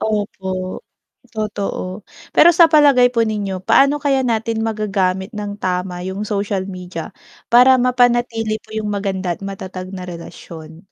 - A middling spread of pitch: Yes, average, 3.8 semitones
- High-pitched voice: Yes, high, 205 Hz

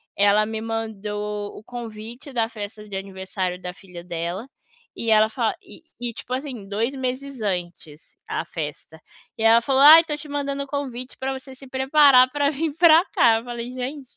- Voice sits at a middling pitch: No, high, 230 Hz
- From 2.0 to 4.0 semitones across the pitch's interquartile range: No, average, 4.7 semitones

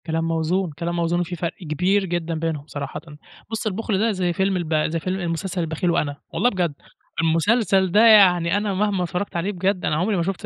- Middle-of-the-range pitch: Yes, medium, 180 Hz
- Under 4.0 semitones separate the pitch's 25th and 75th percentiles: Yes, average, 2.9 semitones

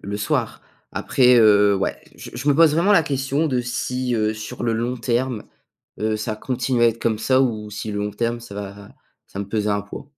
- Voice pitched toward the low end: Yes, low, 115 Hz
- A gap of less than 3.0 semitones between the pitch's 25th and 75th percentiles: No, average, 3.3 semitones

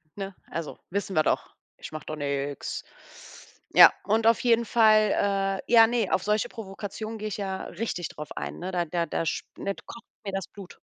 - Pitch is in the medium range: No, high, 195 Hz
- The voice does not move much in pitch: No, average, 3.7 semitones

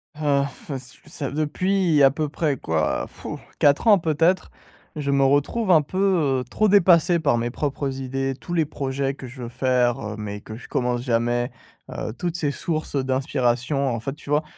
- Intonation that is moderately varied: Yes, average, 3.6 semitones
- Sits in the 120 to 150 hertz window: Yes, medium, 140 Hz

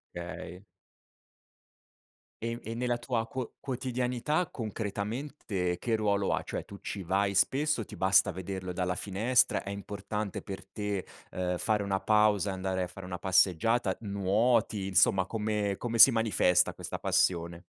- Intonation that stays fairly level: No, average, 3.4 semitones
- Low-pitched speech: Yes, low, 100 Hz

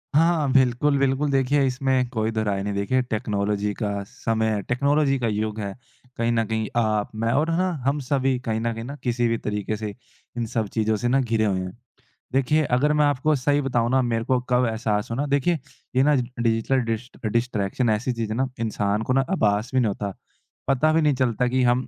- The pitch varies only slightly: No, average, 3.6 semitones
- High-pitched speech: No, low, 120 Hz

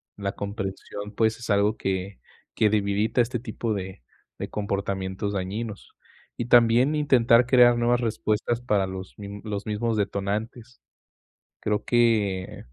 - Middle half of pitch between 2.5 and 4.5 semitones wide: Yes, average, 2.9 semitones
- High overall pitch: No, low, 105 Hz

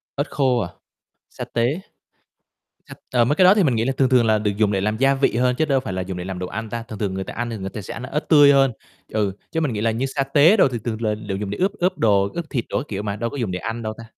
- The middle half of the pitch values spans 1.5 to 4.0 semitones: No, average, 4.5 semitones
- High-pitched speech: No, low, 115 Hz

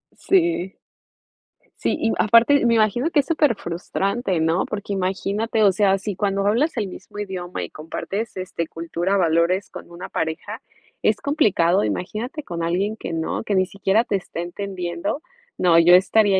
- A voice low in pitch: No, high, 195 Hz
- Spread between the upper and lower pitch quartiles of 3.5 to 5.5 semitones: Yes, average, 3.9 semitones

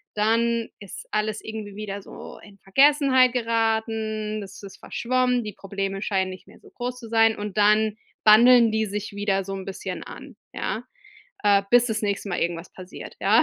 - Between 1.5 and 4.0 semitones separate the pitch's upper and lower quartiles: Yes, narrow, 2.4 semitones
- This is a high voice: Yes, high, 215 Hz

